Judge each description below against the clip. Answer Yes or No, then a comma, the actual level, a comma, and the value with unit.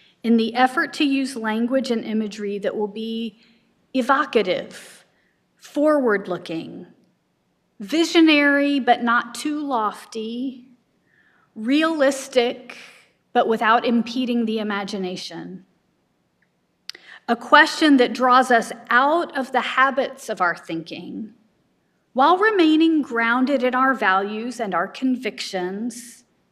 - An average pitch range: Yes, average, 4.0 semitones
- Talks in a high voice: Yes, high, 235 Hz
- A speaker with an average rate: No, slow, 105 wpm